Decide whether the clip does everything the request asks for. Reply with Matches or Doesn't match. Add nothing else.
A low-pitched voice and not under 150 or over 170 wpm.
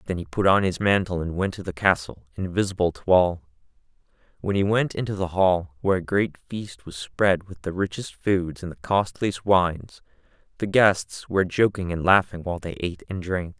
Doesn't match